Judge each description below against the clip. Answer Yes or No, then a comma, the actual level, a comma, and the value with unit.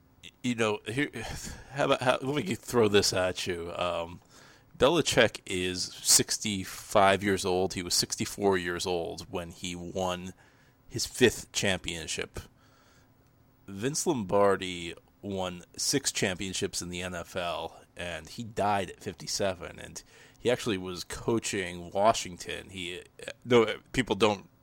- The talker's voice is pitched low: Yes, very low, 95 Hz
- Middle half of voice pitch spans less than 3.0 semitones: No, average, 4.3 semitones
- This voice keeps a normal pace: No, slow, 125 wpm